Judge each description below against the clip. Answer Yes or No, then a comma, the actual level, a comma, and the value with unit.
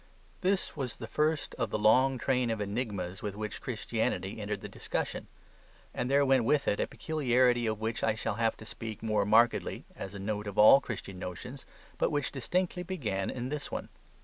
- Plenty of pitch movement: No, average, 4.3 semitones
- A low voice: Yes, low, 115 Hz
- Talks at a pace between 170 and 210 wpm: Yes, average, 195 wpm